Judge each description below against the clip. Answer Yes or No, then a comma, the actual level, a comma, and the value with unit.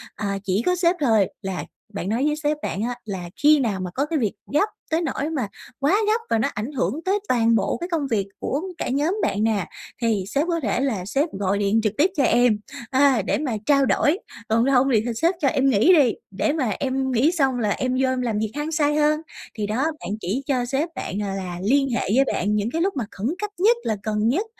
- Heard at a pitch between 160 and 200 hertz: No, very high, 255 Hz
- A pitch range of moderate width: No, wide, 5.9 semitones